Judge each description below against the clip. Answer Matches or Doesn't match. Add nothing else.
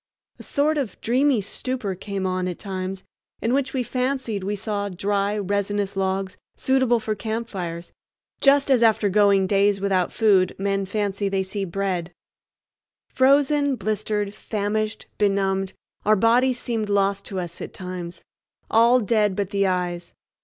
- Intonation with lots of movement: Doesn't match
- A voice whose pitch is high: Matches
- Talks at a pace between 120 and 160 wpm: Matches